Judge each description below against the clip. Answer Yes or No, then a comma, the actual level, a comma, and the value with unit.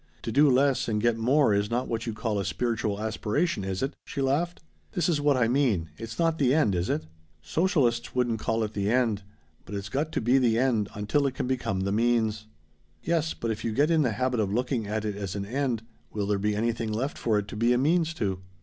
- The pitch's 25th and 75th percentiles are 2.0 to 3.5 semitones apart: No, average, 4.4 semitones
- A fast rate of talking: Yes, fast, 240 wpm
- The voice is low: Yes, low, 115 Hz